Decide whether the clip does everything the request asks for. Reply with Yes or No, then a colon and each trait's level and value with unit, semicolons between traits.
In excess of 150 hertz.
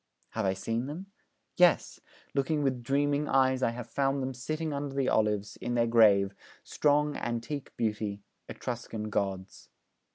No: low, 125 Hz